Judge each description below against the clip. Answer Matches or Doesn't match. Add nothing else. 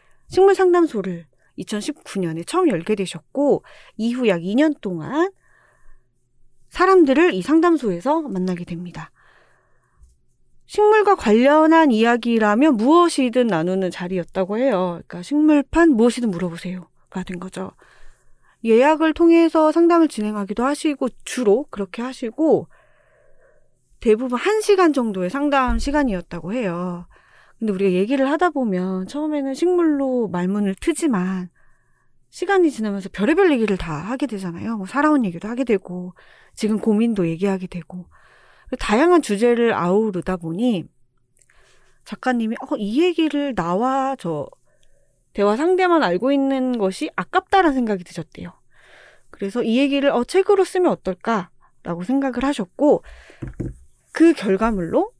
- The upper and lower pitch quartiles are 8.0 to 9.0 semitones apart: Matches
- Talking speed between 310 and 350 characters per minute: Doesn't match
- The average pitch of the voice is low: Doesn't match